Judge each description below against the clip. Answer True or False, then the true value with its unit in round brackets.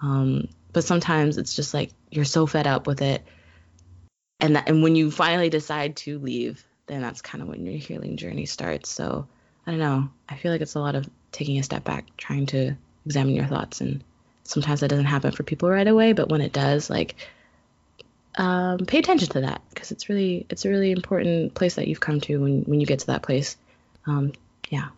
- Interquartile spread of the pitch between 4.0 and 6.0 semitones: False (3.4 semitones)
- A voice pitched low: False (150 Hz)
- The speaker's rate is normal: False (215 wpm)